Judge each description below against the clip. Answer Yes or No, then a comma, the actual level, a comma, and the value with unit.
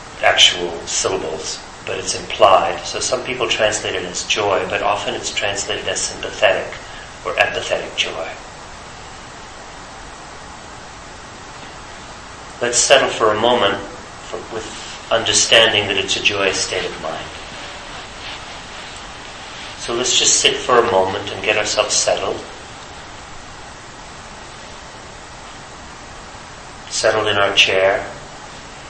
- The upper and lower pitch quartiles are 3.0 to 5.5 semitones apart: Yes, average, 3.5 semitones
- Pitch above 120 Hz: No, low, 110 Hz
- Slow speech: Yes, slow, 105 wpm